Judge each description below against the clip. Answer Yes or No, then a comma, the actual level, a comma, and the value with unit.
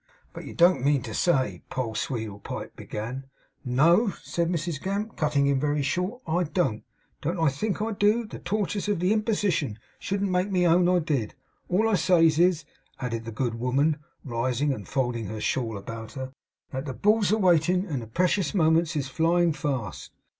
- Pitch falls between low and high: Yes, medium, 160 Hz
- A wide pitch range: Yes, wide, 5.9 semitones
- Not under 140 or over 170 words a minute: No, average, 185 wpm